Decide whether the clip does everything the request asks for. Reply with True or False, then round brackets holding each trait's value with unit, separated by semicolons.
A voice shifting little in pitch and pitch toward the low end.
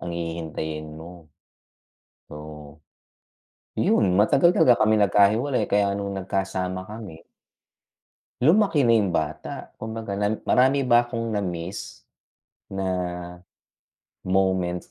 False (4.2 semitones; 95 Hz)